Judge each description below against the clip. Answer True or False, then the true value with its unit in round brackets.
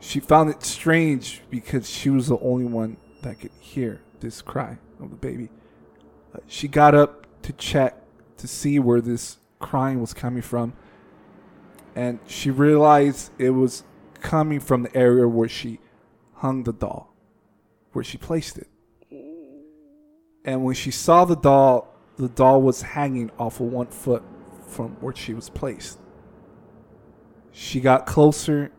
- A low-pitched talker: True (130 Hz)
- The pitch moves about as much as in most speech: True (3.6 semitones)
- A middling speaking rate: True (150 wpm)